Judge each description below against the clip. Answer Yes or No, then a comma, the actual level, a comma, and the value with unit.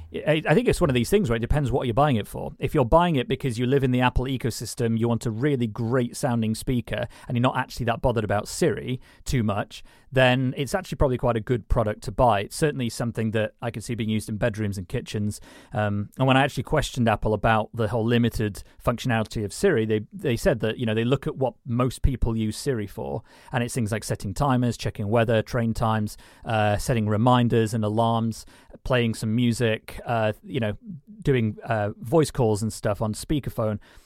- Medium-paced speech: No, fast, 220 wpm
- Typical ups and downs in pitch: Yes, average, 3.0 semitones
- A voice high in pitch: No, low, 120 Hz